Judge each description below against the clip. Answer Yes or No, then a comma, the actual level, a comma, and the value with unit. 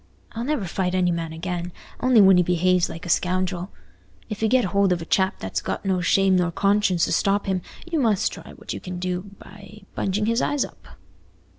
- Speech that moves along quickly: Yes, fast, 210 wpm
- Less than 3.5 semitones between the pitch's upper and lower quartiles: Yes, narrow, 2.5 semitones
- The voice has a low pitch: No, medium, 185 Hz